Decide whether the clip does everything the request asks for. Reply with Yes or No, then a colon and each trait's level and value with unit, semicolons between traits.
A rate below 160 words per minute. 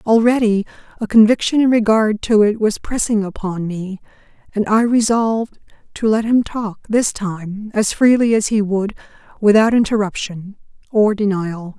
Yes: average, 150 wpm